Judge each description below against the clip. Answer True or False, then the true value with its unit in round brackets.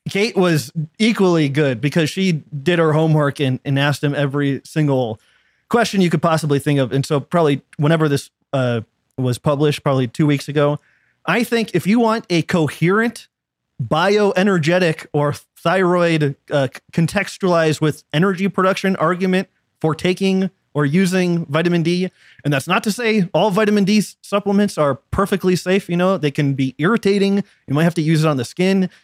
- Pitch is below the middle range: False (165 Hz)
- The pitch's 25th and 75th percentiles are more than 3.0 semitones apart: True (4.6 semitones)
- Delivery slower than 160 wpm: False (170 wpm)